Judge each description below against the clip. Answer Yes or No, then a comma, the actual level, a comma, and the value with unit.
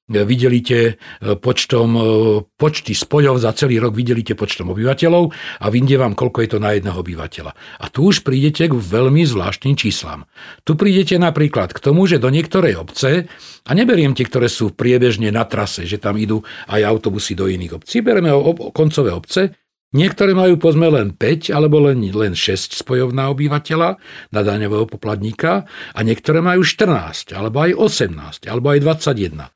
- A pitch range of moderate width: No, wide, 6.5 semitones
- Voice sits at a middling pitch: No, low, 125 Hz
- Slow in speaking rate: No, fast, 165 wpm